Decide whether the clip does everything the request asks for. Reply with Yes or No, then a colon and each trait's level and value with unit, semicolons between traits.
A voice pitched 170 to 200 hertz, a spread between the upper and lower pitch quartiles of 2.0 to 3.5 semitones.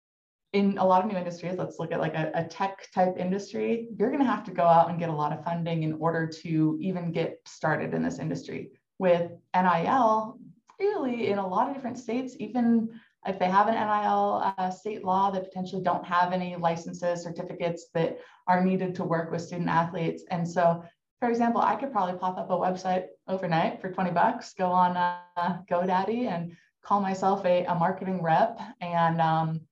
Yes: medium, 185 Hz; average, 2.9 semitones